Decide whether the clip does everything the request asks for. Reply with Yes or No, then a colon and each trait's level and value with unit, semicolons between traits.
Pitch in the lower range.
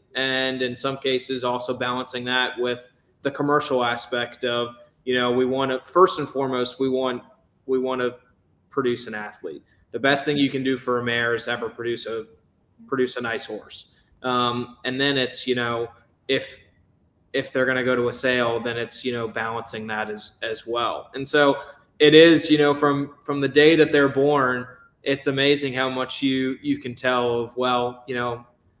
Yes: low, 125 Hz